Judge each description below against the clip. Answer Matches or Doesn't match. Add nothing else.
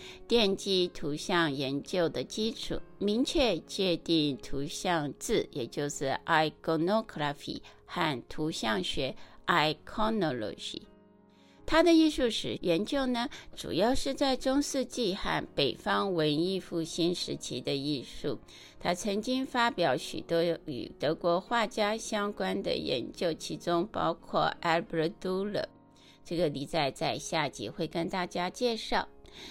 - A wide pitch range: Matches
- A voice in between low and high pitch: Matches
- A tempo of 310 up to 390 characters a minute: Doesn't match